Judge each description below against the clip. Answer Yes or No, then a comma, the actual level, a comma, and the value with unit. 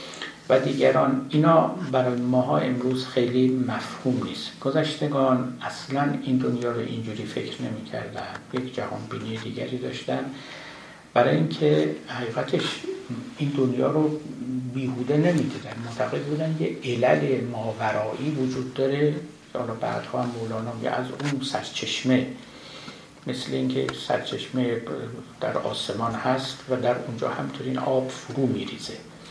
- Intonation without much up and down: Yes, narrow, 2.3 semitones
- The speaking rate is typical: Yes, average, 125 wpm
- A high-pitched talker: No, low, 130 Hz